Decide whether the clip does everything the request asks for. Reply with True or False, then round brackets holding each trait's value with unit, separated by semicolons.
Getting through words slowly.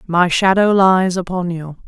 False (160 wpm)